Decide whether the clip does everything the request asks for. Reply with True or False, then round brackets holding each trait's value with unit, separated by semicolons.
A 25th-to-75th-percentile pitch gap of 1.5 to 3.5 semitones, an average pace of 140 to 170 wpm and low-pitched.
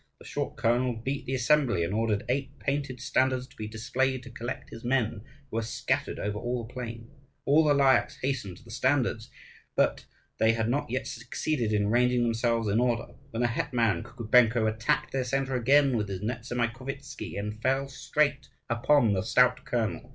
False (2.9 semitones; 180 wpm; 120 Hz)